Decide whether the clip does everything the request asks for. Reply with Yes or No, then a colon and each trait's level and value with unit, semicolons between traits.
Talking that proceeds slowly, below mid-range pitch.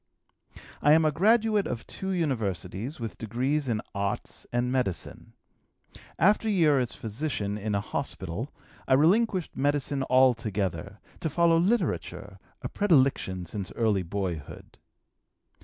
Yes: slow, 125 wpm; low, 130 Hz